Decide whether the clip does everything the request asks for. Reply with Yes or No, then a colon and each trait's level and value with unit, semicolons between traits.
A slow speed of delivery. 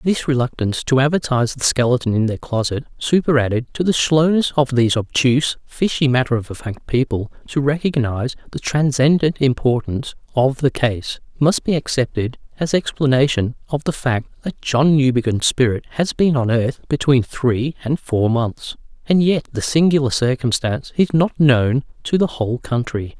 No: average, 160 wpm